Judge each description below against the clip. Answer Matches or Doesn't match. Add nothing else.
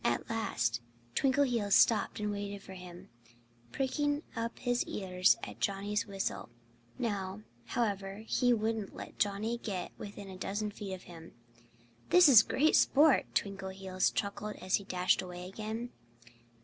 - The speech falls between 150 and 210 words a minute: Doesn't match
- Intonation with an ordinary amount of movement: Matches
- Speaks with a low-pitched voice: Doesn't match